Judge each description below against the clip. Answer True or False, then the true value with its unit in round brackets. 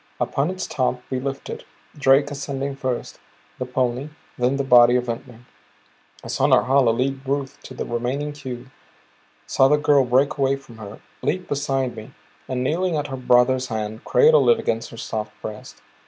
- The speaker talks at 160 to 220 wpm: True (170 wpm)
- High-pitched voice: False (130 Hz)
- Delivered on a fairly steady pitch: True (2.3 semitones)